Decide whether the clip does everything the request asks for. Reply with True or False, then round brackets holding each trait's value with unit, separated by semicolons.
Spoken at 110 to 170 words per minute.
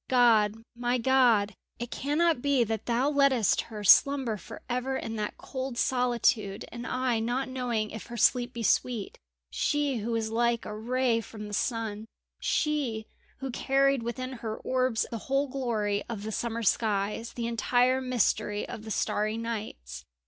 True (165 wpm)